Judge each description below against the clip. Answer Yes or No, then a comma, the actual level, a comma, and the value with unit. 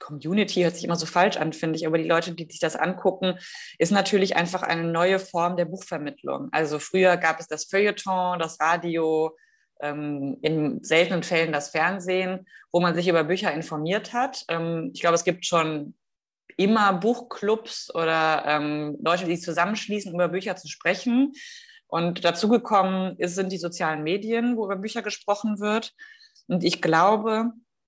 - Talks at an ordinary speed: Yes, average, 160 wpm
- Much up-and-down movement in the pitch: No, average, 3.8 semitones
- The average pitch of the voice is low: No, medium, 175 Hz